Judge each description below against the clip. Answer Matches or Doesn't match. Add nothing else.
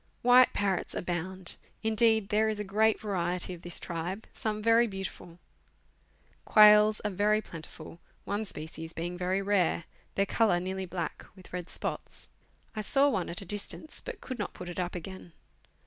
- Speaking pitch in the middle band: Doesn't match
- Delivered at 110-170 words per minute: Matches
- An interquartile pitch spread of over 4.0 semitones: Doesn't match